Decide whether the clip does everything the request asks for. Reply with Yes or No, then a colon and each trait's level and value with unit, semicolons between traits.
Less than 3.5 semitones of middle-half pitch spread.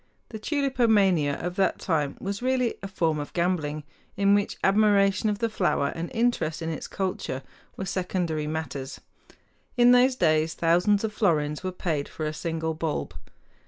No: average, 4.7 semitones